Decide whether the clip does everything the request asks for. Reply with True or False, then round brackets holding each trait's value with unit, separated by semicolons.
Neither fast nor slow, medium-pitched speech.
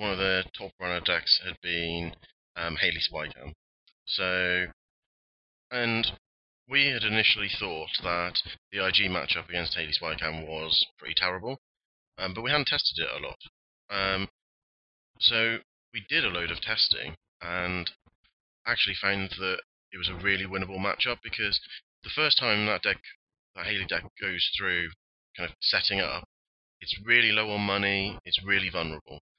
False (155 wpm; 95 Hz)